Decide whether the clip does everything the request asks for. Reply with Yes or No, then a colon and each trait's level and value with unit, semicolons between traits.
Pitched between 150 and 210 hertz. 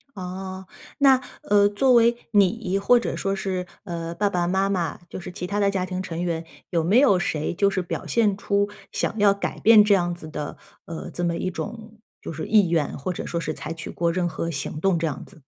Yes: medium, 185 Hz